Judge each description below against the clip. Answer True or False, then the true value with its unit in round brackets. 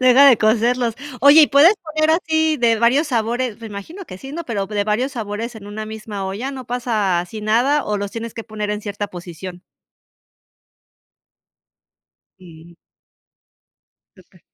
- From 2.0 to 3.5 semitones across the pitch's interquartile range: False (4.1 semitones)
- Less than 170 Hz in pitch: False (225 Hz)